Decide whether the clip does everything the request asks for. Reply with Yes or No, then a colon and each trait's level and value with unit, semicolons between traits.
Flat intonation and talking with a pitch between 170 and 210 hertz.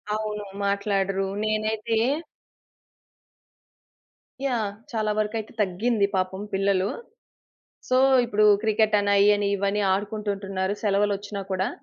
Yes: narrow, 1.5 semitones; high, 205 Hz